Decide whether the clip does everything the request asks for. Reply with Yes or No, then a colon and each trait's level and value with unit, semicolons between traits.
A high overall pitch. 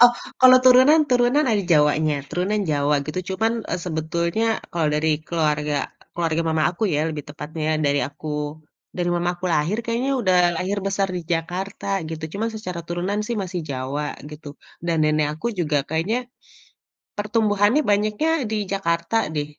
No: medium, 175 Hz